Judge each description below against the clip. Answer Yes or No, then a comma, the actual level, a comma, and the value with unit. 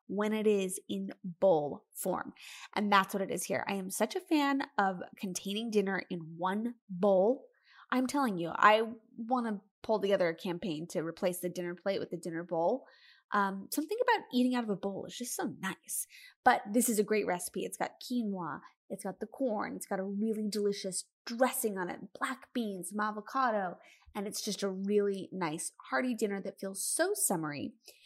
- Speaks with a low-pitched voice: No, high, 205 Hz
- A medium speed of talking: Yes, average, 190 wpm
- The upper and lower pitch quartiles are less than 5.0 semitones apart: Yes, average, 4.0 semitones